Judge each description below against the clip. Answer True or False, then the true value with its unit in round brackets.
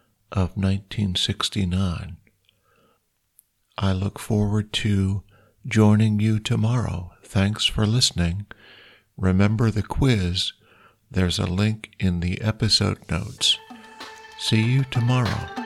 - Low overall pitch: True (105 Hz)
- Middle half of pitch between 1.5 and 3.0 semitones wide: True (2.7 semitones)